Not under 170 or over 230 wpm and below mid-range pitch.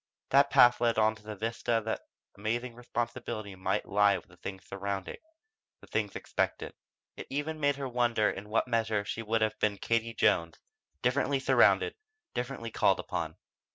No: average, 160 wpm; low, 115 Hz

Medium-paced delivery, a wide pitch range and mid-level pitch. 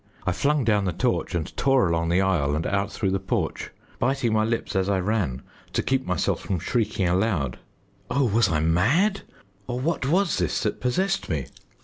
No: average, 195 wpm; wide, 6.3 semitones; low, 100 Hz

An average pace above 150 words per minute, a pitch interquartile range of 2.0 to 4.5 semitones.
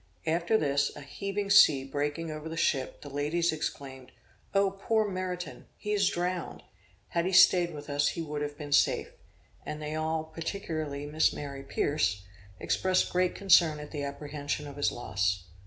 Yes: average, 170 wpm; average, 3.7 semitones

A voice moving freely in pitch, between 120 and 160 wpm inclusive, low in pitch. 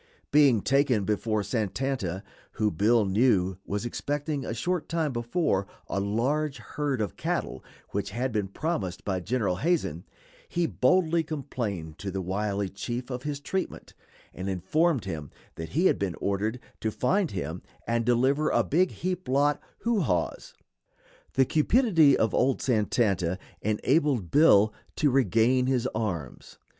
Yes: wide, 6.7 semitones; average, 145 wpm; low, 120 Hz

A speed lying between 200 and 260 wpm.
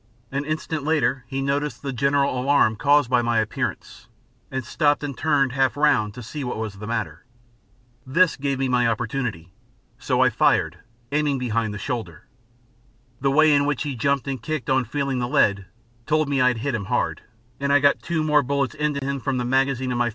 Yes: fast, 205 wpm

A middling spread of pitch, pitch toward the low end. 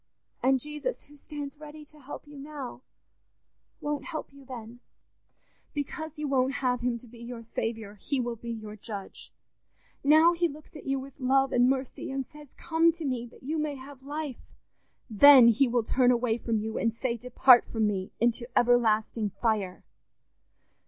No: average, 3.8 semitones; very high, 255 Hz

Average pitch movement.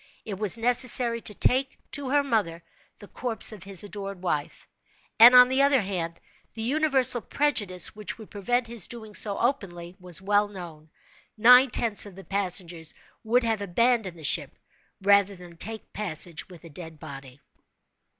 Yes: average, 5.0 semitones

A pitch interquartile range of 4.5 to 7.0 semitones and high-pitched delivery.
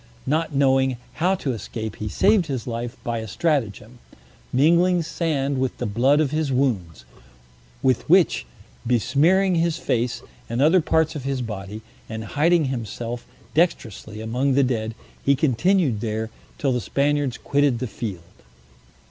No: average, 5.2 semitones; low, 130 Hz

